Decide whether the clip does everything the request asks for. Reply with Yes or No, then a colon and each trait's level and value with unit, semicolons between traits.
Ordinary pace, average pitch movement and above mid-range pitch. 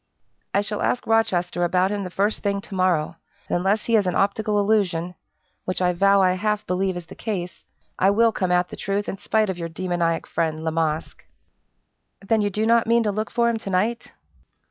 No: fast, 210 wpm; average, 3.1 semitones; high, 195 Hz